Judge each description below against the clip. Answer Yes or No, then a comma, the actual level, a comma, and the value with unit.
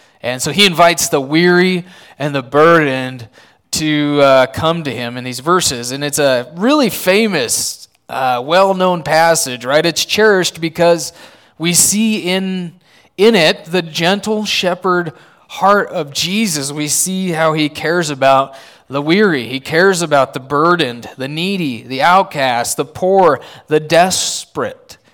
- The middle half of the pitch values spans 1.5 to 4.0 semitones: No, average, 4.5 semitones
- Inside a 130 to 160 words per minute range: Yes, average, 150 wpm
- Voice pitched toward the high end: No, medium, 165 Hz